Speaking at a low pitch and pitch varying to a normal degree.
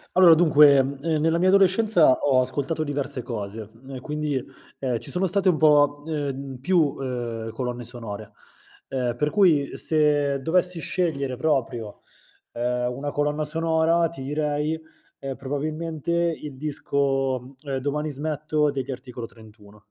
No: medium, 145 Hz; average, 3.5 semitones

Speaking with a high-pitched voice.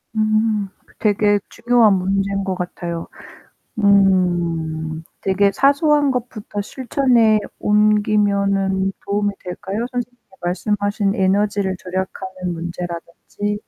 Yes: high, 200 Hz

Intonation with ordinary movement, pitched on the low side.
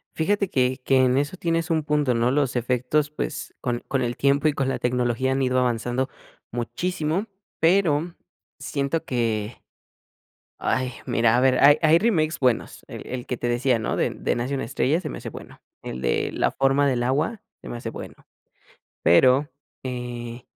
Yes: average, 3.7 semitones; low, 130 Hz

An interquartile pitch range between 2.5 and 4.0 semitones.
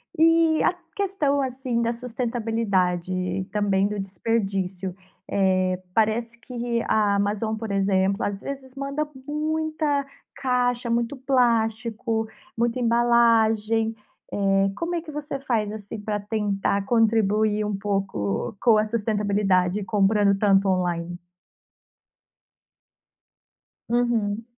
Yes: average, 3.5 semitones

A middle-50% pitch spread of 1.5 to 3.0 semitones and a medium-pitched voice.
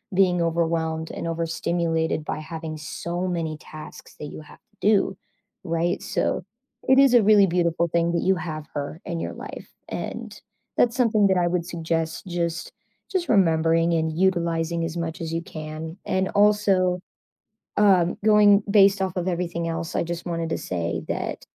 Yes: narrow, 2.5 semitones; medium, 170 Hz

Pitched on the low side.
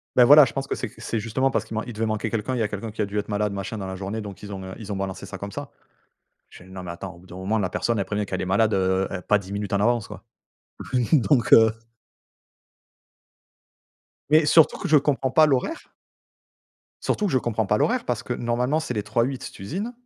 Yes: low, 110 Hz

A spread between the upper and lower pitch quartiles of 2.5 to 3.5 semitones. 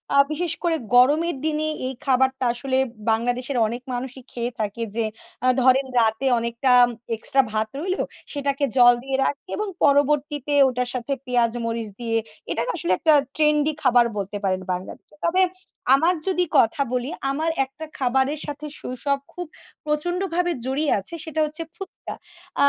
No: average, 4.0 semitones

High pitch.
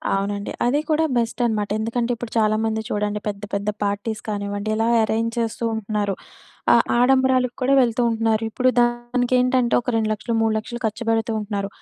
Yes: high, 225 Hz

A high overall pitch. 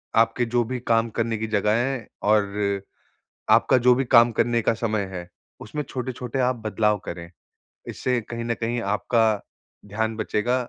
No: low, 115 Hz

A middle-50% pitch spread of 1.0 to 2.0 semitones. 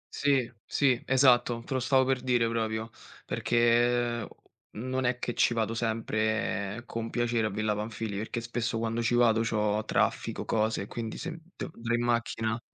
Yes: narrow, 1.6 semitones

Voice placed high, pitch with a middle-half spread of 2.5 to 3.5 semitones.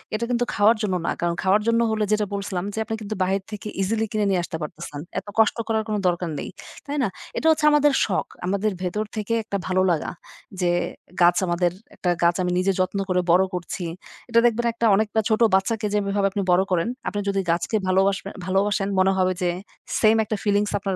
Yes: high, 200 Hz; average, 2.9 semitones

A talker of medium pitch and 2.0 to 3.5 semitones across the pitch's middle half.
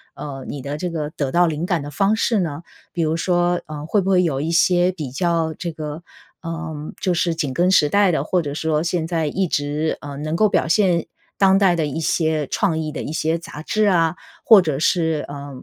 Yes: medium, 165 Hz; average, 2.8 semitones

